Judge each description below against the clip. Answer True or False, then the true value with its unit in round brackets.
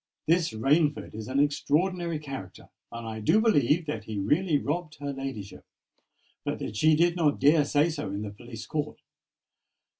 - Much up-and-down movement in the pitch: True (6.0 semitones)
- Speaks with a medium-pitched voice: True (145 Hz)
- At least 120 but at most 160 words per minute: False (170 wpm)